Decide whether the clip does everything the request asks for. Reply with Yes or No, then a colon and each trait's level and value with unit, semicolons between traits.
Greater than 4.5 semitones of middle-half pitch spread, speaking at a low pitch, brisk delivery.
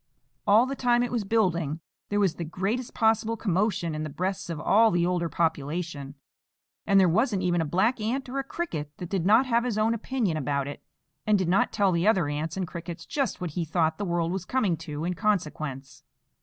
No: average, 5.2 semitones; medium, 185 Hz; fast, 215 wpm